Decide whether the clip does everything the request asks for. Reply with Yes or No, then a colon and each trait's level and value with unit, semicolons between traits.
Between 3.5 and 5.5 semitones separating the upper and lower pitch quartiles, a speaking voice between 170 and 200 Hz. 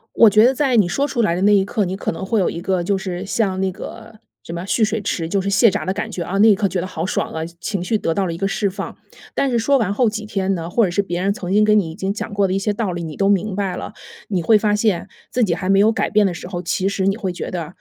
No: average, 2.8 semitones; high, 195 Hz